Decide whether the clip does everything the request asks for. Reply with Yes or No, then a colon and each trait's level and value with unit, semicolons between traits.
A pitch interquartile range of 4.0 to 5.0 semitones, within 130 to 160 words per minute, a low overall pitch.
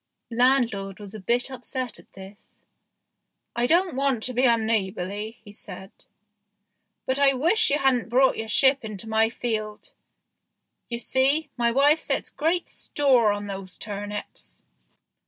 No: average, 4.3 semitones; average, 150 wpm; high, 235 Hz